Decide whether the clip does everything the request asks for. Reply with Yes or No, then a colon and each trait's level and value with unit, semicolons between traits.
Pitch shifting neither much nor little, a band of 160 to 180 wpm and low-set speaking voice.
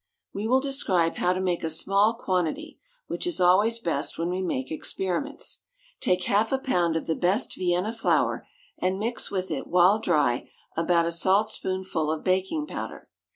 No: average, 4.2 semitones; average, 175 wpm; medium, 185 Hz